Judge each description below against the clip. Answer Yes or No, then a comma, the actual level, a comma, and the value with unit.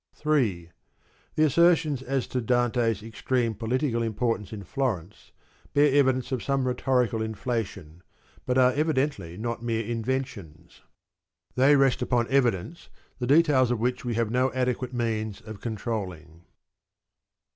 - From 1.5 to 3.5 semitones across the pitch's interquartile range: Yes, average, 3.2 semitones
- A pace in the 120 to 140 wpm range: Yes, slow, 135 wpm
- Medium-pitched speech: No, low, 120 Hz